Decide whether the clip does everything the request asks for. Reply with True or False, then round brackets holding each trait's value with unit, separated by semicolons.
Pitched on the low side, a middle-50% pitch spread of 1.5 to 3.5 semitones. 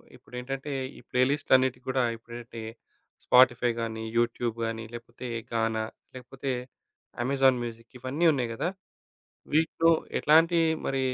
True (125 Hz; 2.6 semitones)